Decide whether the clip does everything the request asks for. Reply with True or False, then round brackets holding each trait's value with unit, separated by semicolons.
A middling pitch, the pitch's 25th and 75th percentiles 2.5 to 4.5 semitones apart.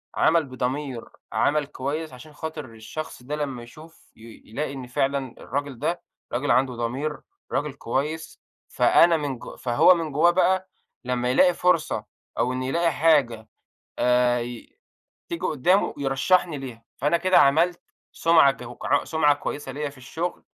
True (145 Hz; 4.1 semitones)